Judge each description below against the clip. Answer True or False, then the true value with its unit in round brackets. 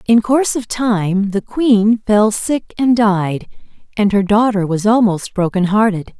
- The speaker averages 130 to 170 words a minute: True (165 wpm)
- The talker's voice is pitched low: False (210 Hz)